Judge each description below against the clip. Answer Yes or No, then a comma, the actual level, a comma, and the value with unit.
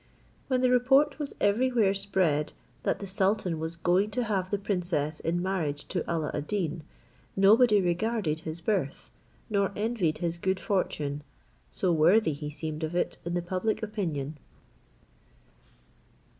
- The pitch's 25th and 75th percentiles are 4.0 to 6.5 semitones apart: Yes, average, 4.6 semitones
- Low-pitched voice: No, medium, 185 Hz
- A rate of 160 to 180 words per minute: No, average, 145 wpm